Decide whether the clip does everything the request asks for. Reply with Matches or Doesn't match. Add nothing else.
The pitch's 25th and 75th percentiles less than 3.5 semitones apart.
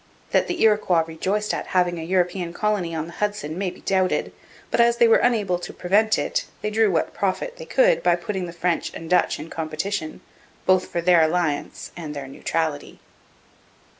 Doesn't match